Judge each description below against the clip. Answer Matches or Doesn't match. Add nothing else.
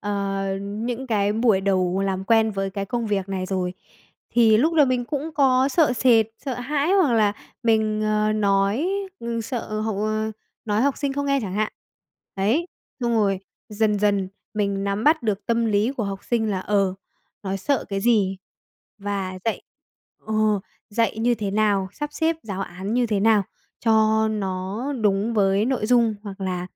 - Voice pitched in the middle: Doesn't match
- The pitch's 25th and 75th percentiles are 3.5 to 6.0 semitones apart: Doesn't match